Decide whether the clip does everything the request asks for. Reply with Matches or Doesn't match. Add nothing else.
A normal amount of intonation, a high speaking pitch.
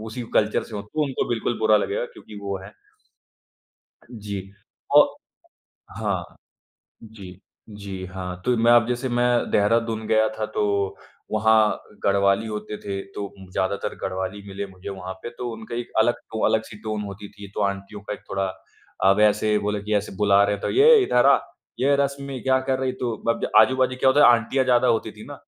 Doesn't match